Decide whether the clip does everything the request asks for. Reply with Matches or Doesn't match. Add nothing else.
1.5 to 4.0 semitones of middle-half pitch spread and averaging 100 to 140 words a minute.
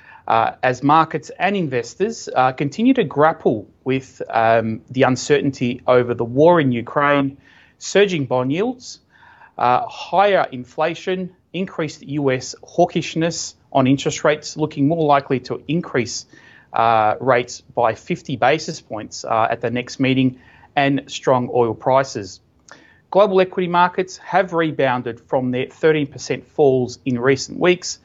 Doesn't match